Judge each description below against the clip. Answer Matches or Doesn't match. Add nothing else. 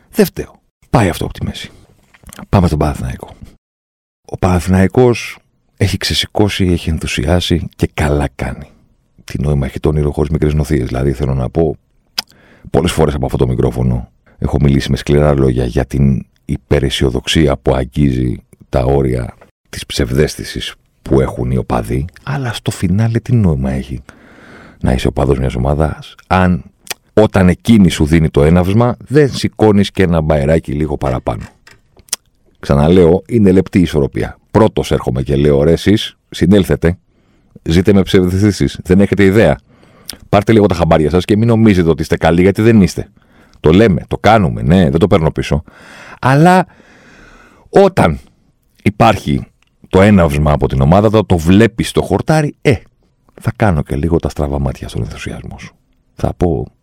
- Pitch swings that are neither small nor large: Doesn't match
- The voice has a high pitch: Doesn't match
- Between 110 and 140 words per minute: Doesn't match